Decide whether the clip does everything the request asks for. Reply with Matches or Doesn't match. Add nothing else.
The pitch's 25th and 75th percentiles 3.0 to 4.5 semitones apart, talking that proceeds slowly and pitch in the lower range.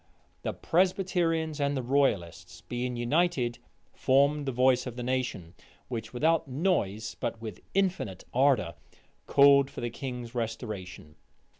Matches